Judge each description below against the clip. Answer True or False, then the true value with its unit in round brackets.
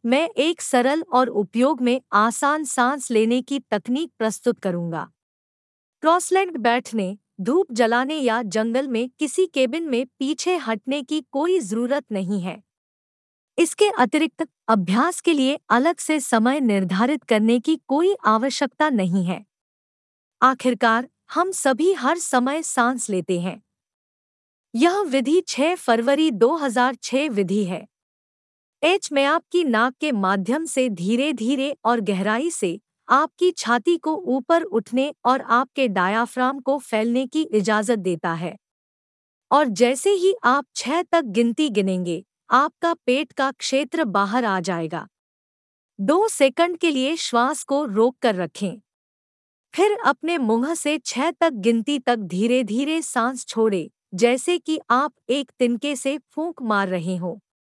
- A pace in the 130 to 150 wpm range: True (135 wpm)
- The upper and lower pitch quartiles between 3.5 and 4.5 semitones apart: False (5.3 semitones)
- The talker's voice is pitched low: False (255 Hz)